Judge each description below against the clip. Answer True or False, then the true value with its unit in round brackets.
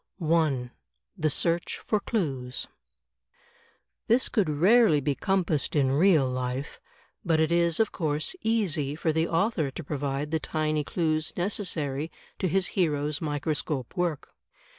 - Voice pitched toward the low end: False (155 Hz)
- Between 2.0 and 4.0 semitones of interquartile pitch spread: True (3.4 semitones)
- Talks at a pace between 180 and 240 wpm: False (140 wpm)